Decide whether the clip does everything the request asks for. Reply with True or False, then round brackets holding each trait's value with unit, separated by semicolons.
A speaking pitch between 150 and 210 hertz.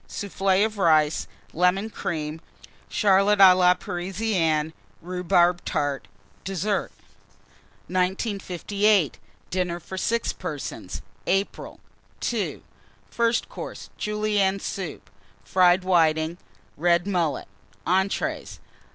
True (185 Hz)